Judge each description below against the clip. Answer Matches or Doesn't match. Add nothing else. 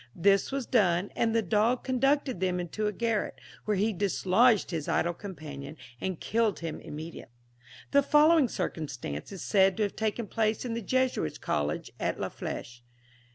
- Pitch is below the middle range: Doesn't match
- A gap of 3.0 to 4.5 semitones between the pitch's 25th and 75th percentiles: Doesn't match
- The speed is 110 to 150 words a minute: Doesn't match